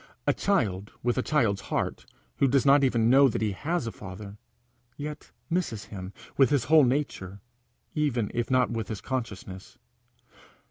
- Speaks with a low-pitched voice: Yes, low, 120 Hz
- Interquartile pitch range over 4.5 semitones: Yes, wide, 5.4 semitones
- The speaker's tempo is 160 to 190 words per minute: Yes, average, 165 wpm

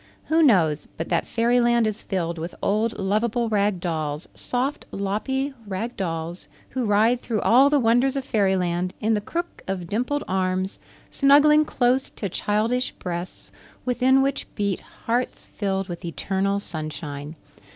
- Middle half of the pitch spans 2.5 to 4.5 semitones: No, average, 5.2 semitones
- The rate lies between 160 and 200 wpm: No, average, 145 wpm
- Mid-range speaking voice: No, high, 210 Hz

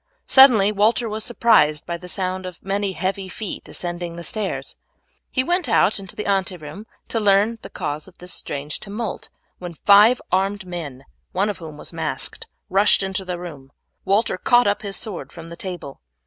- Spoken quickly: No, average, 185 wpm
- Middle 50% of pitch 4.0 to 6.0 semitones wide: No, average, 3.3 semitones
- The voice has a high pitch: Yes, high, 195 Hz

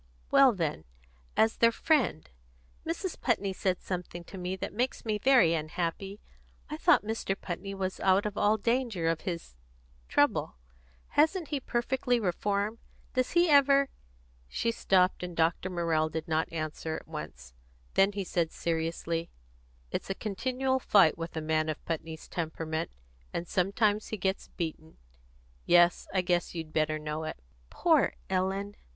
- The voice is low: No, medium, 185 Hz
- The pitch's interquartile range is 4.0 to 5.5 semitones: Yes, average, 5.0 semitones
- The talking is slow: No, average, 155 wpm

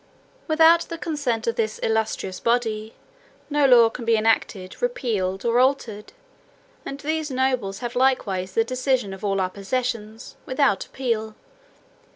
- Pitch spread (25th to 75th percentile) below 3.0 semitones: No, average, 3.7 semitones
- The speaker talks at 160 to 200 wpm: No, average, 140 wpm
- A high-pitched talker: Yes, high, 230 Hz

